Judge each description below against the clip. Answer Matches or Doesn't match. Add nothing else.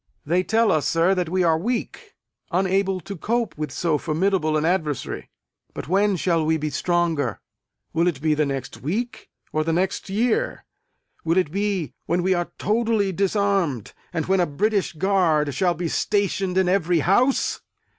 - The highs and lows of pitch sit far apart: Doesn't match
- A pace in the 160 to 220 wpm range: Matches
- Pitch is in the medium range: Matches